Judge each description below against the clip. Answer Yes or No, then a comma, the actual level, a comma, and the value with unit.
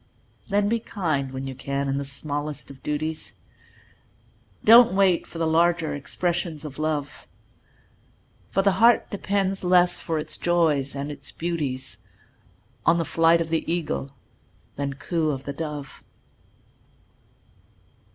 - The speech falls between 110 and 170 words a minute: Yes, slow, 135 wpm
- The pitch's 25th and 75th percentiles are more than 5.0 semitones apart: No, average, 3.7 semitones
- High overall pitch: No, medium, 160 Hz